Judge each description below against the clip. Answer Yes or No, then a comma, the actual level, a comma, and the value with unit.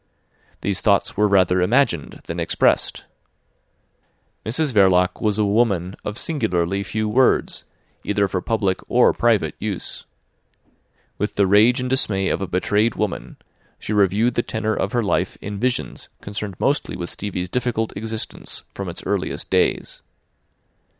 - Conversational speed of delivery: Yes, average, 145 wpm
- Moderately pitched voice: No, low, 105 Hz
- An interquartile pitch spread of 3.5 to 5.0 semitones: No, narrow, 2.6 semitones